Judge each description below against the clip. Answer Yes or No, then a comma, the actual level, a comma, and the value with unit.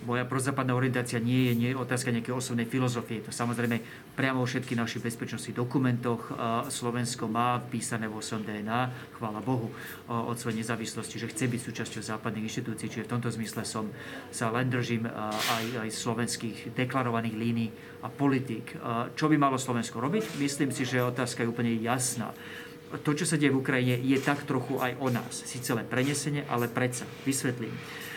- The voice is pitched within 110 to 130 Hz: Yes, low, 120 Hz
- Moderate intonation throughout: No, narrow, 1.9 semitones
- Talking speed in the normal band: No, fast, 175 wpm